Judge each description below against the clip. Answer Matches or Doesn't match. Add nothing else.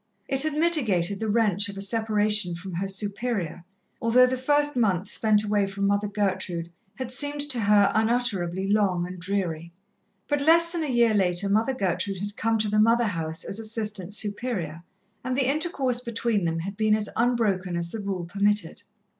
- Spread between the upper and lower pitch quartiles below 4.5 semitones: Matches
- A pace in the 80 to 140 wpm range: Doesn't match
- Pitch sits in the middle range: Doesn't match